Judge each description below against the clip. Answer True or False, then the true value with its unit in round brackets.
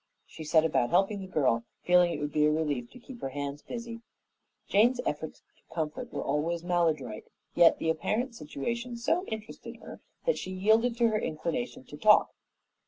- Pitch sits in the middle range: True (175 Hz)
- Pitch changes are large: True (7.3 semitones)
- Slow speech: False (180 wpm)